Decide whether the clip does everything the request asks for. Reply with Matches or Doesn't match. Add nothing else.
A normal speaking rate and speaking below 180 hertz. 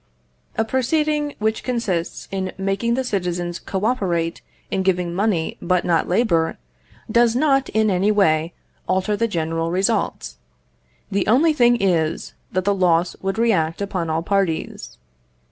Doesn't match